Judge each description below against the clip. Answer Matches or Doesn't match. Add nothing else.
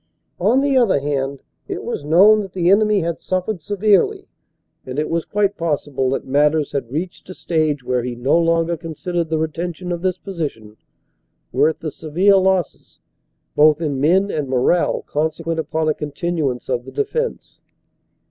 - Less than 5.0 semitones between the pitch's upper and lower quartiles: Matches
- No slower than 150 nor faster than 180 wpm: Matches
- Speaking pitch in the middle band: Matches